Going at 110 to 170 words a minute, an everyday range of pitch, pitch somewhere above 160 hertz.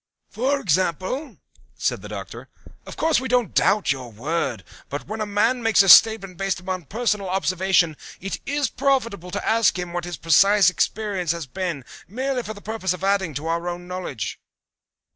No: average, 180 wpm; average, 4.2 semitones; high, 190 Hz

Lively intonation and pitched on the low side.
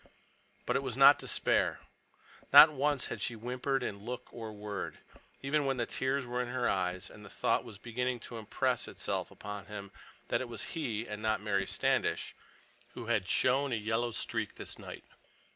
No: average, 3.6 semitones; low, 120 Hz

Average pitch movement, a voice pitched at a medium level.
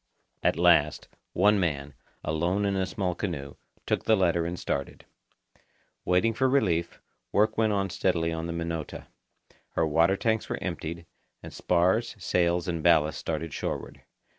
No: average, 3.1 semitones; very low, 85 Hz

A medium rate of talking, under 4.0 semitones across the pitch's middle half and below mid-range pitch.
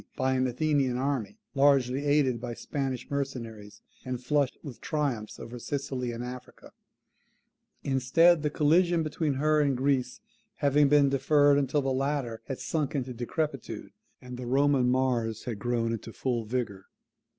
Yes: average, 150 wpm; average, 2.8 semitones; low, 130 Hz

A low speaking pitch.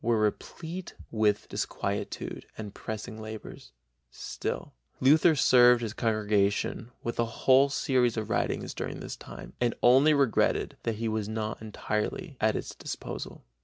Yes: low, 115 Hz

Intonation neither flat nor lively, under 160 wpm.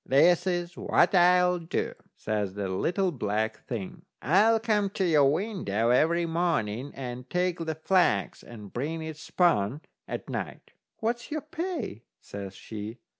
No: wide, 8.1 semitones; average, 145 wpm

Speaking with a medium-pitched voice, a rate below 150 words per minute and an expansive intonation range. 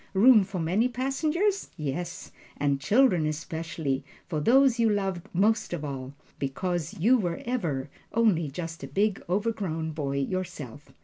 Yes: medium, 175 Hz; average, 140 wpm; wide, 6.4 semitones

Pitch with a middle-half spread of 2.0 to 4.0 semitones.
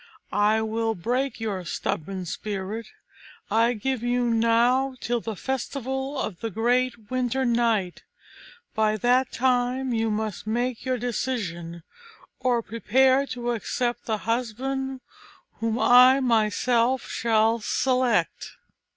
Yes: average, 2.7 semitones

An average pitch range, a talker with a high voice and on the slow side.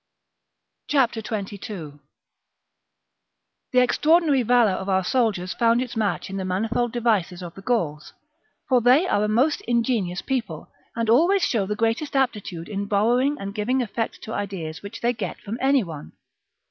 No: average, 4.1 semitones; high, 225 Hz; average, 160 wpm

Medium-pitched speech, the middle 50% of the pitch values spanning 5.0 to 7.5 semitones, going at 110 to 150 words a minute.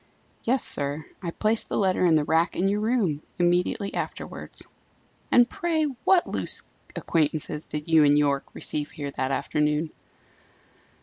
Yes: medium, 160 Hz; average, 5.3 semitones; average, 145 wpm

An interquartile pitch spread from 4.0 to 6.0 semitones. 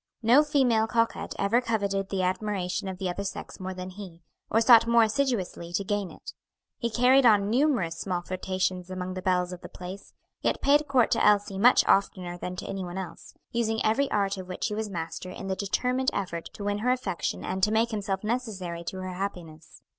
No: average, 3.6 semitones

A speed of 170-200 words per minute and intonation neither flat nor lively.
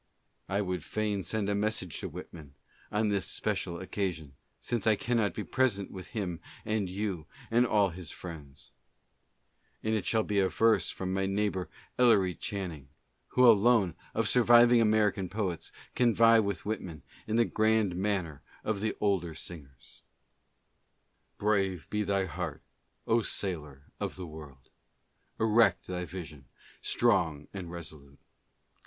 No: average, 150 wpm; average, 4.0 semitones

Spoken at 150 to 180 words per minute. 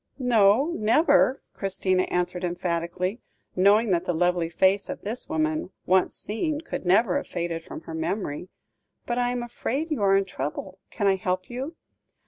Yes: average, 165 wpm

